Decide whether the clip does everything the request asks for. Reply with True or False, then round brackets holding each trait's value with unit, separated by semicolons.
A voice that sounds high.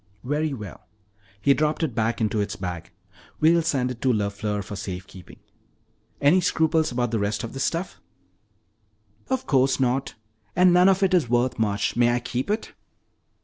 False (125 Hz)